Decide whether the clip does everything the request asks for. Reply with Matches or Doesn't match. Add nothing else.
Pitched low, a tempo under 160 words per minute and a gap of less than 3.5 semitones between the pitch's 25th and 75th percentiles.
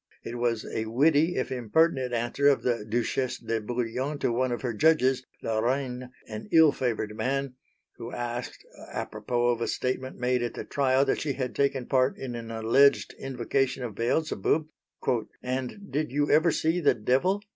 Doesn't match